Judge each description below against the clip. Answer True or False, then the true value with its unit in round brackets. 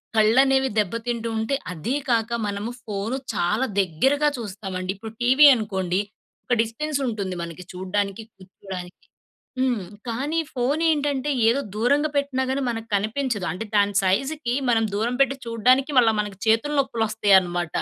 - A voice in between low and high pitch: False (225 Hz)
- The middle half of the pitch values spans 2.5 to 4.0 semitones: False (5.0 semitones)